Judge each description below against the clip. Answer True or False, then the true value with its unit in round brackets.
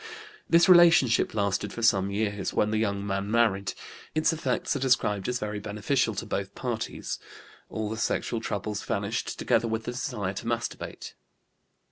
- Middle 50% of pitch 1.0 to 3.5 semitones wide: True (3.2 semitones)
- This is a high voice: False (110 Hz)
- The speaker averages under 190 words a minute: True (160 wpm)